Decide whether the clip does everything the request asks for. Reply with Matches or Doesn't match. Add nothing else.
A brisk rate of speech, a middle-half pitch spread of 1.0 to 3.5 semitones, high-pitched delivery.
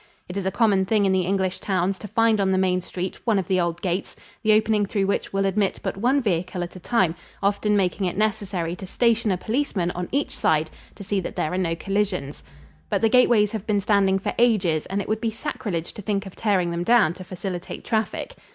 Matches